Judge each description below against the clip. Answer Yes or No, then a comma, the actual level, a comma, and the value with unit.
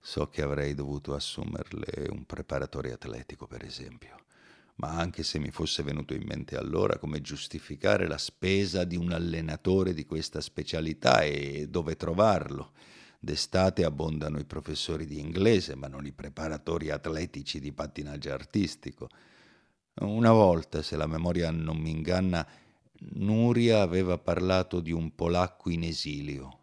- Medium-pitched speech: No, very low, 80 Hz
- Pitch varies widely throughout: No, average, 3.3 semitones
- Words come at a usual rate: Yes, average, 140 wpm